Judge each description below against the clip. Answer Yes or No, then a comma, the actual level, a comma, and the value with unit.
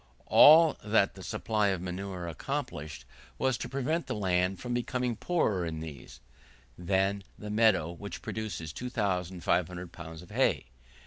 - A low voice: Yes, very low, 95 Hz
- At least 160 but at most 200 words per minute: No, average, 140 wpm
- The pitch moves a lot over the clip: No, average, 4.2 semitones